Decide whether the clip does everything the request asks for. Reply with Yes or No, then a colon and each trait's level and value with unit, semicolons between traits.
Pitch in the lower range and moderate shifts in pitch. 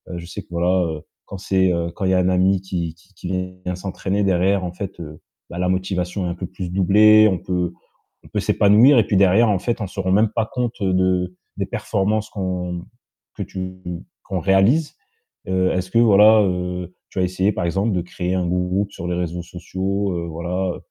No: very low, 95 Hz; narrow, 1.8 semitones